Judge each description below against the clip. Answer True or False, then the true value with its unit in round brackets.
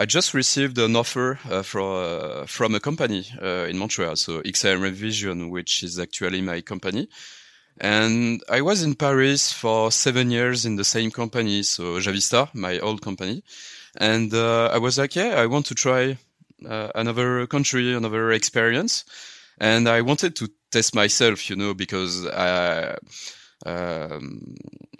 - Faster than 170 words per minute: False (155 wpm)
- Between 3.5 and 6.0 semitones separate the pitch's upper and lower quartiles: True (4.2 semitones)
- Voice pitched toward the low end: True (115 Hz)